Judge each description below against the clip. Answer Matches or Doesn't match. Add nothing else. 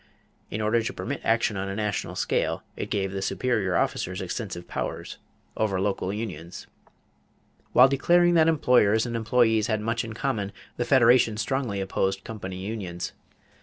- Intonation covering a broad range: Doesn't match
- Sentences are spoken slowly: Doesn't match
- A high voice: Doesn't match